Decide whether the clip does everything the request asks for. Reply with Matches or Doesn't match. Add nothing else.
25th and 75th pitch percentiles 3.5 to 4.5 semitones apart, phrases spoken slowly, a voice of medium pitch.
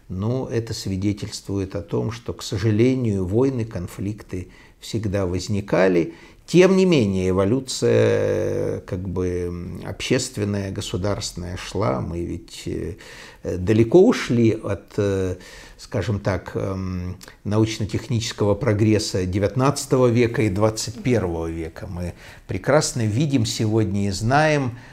Doesn't match